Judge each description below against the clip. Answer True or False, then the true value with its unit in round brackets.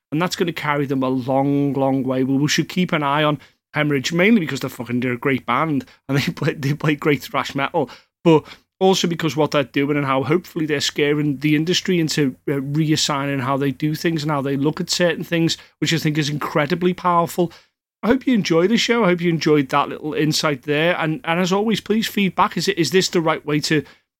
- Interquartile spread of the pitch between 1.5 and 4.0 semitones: True (3.7 semitones)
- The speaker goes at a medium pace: False (230 wpm)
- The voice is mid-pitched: True (155 Hz)